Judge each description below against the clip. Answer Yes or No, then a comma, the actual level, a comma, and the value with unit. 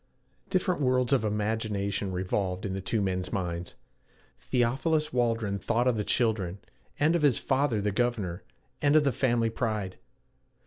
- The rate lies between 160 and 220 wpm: No, average, 150 wpm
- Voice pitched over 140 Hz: No, low, 110 Hz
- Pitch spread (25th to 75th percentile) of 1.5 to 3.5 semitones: No, average, 4.5 semitones